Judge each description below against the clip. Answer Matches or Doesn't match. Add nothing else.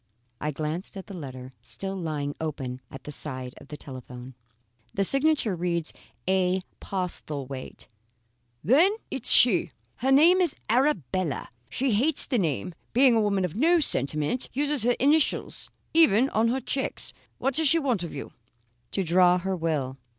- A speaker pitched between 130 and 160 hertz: Doesn't match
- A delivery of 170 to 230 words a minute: Doesn't match